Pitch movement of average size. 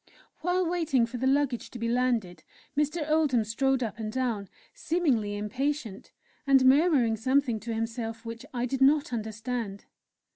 Yes: average, 3.8 semitones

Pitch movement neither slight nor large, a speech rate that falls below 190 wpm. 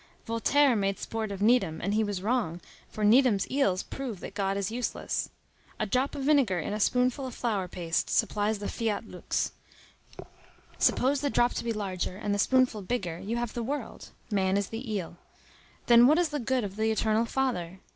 No: average, 4.1 semitones; average, 195 wpm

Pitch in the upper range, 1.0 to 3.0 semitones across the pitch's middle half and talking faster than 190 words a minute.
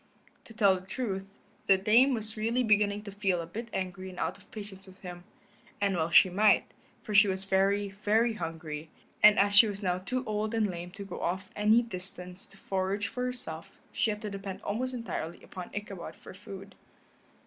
Yes: high, 200 Hz; narrow, 2.4 semitones; average, 200 wpm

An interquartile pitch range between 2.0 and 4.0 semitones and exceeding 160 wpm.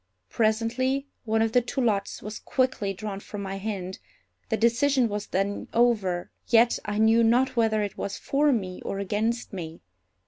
Yes: average, 3.1 semitones; average, 170 wpm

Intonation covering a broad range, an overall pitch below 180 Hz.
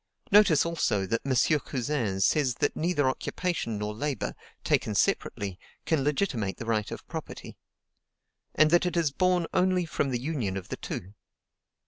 Yes: wide, 7.3 semitones; medium, 140 Hz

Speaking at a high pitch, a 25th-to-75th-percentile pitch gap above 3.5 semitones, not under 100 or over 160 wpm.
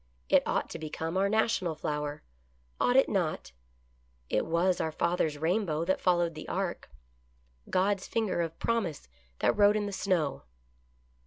No: medium, 175 Hz; average, 4.2 semitones; average, 155 wpm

